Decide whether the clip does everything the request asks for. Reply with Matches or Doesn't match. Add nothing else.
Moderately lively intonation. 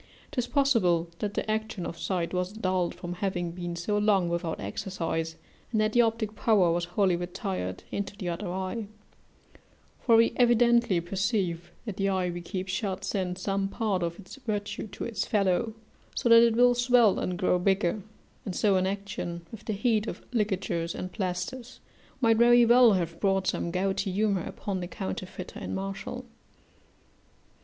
Matches